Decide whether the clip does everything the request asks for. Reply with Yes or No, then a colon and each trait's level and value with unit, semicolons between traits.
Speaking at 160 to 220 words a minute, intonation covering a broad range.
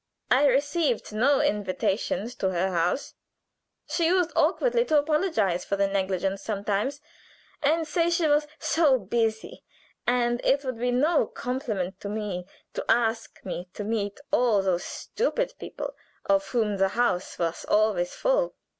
No: average, 145 wpm; wide, 6.8 semitones